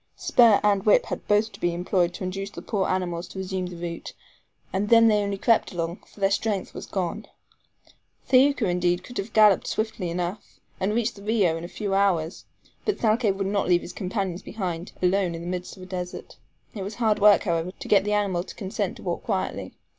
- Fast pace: Yes, fast, 215 wpm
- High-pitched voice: Yes, high, 195 Hz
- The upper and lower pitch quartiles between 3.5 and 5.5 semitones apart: No, average, 2.8 semitones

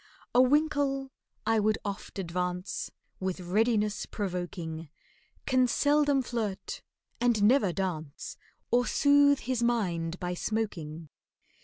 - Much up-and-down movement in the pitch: Yes, wide, 5.9 semitones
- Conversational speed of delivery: No, slow, 110 wpm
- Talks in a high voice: Yes, high, 210 Hz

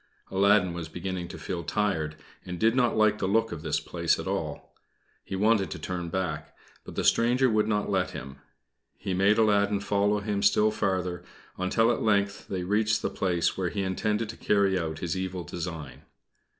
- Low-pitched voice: Yes, very low, 95 Hz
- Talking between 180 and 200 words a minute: Yes, average, 190 wpm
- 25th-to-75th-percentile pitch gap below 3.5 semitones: Yes, average, 3.0 semitones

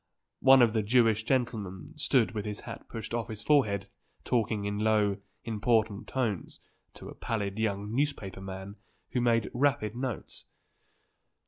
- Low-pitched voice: Yes, low, 110 Hz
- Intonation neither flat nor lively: Yes, average, 3.0 semitones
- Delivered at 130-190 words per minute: Yes, average, 145 wpm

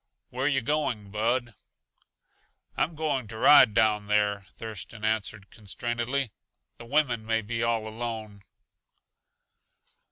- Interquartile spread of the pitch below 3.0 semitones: Yes, narrow, 2.6 semitones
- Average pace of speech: No, slow, 115 wpm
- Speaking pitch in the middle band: No, low, 115 Hz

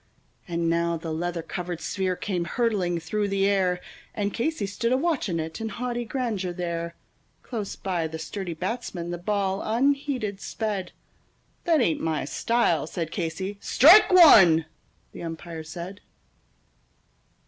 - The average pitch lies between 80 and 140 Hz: No, high, 190 Hz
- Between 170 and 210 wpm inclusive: No, average, 140 wpm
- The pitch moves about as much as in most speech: Yes, average, 4.8 semitones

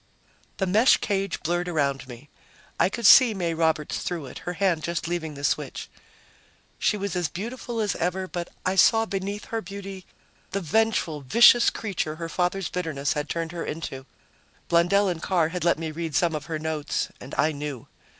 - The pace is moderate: Yes, average, 185 wpm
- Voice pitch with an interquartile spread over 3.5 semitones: Yes, average, 3.9 semitones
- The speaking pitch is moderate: Yes, medium, 175 Hz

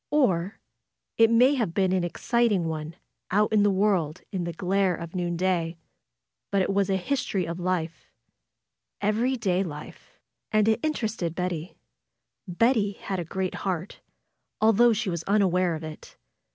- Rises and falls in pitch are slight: No, average, 3.7 semitones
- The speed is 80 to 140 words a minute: No, average, 155 wpm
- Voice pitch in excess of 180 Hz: Yes, high, 190 Hz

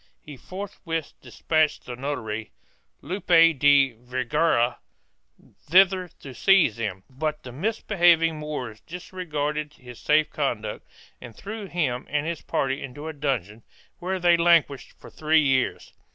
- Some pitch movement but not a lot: Yes, average, 4.8 semitones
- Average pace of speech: No, slow, 130 wpm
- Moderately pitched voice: Yes, medium, 150 Hz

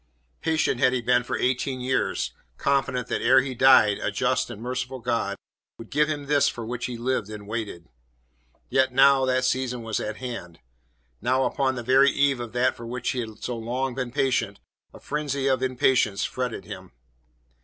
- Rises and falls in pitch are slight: Yes, narrow, 2.2 semitones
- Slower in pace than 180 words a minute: No, average, 190 wpm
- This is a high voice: No, low, 125 Hz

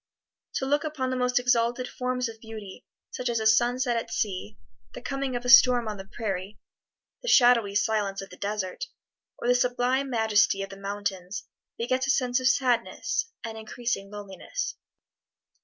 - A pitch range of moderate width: Yes, average, 3.5 semitones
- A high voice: Yes, high, 235 Hz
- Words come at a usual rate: Yes, average, 170 wpm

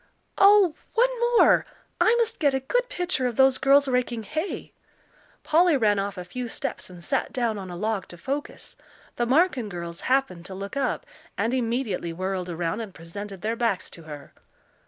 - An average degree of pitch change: No, wide, 7.0 semitones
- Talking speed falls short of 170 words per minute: No, average, 180 wpm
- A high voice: Yes, high, 235 Hz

